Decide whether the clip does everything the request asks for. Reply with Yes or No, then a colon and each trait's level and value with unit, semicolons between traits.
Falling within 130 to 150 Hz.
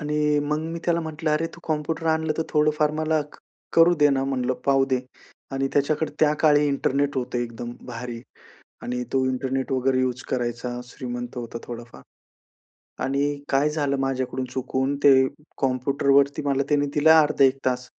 Yes: medium, 140 Hz